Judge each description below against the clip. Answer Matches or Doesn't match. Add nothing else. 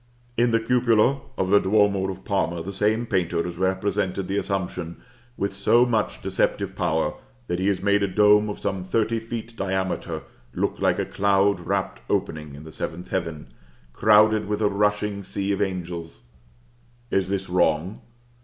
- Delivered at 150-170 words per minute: Matches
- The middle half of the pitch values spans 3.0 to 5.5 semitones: Doesn't match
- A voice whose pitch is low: Matches